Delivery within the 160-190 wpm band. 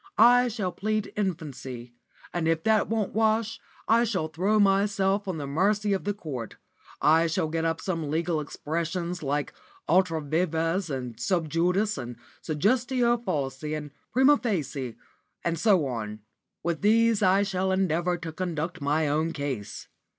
No: average, 150 wpm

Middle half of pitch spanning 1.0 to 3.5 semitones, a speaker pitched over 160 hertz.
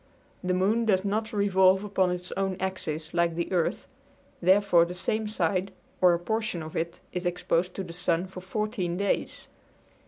Yes: narrow, 2.5 semitones; medium, 185 Hz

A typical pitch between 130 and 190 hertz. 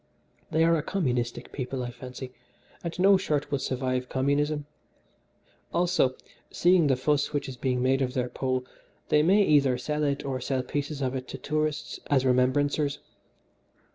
Yes: medium, 140 Hz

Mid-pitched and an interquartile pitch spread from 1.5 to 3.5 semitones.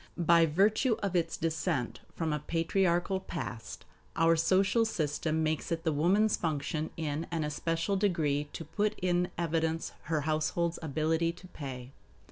Yes: medium, 165 Hz; narrow, 2.4 semitones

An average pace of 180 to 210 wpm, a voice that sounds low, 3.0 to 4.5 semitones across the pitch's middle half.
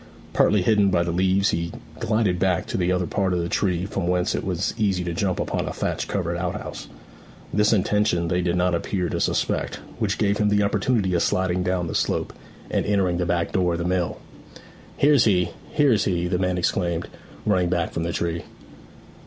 No: fast, 205 wpm; very low, 90 Hz; narrow, 2.4 semitones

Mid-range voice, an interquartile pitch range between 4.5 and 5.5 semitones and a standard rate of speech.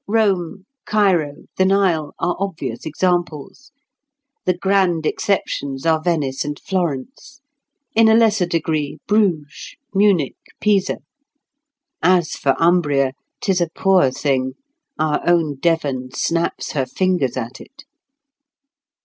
No: medium, 175 Hz; average, 4.9 semitones; slow, 110 wpm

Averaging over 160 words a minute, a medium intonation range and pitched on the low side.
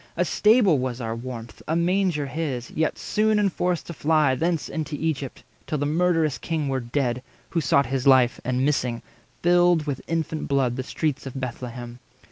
No: average, 175 wpm; average, 4.4 semitones; medium, 145 Hz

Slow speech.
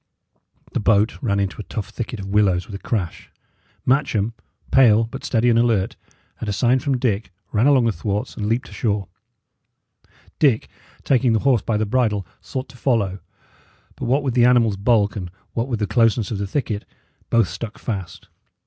No: average, 185 wpm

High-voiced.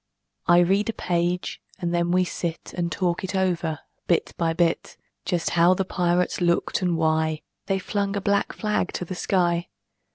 No: medium, 175 Hz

